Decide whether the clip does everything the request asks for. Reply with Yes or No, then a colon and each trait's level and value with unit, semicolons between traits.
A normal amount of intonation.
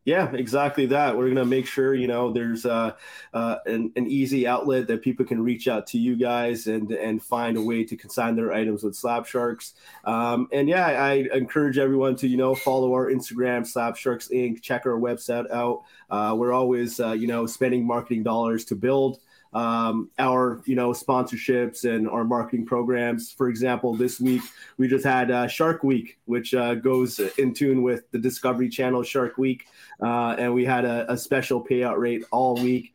No: narrow, 1.6 semitones